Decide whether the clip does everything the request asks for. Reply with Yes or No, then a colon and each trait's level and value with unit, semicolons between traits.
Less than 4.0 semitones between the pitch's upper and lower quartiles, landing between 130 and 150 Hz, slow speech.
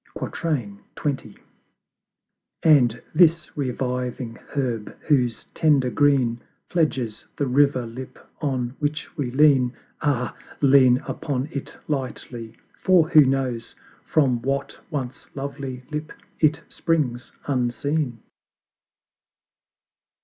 Yes: average, 3.1 semitones; low, 135 Hz; slow, 95 wpm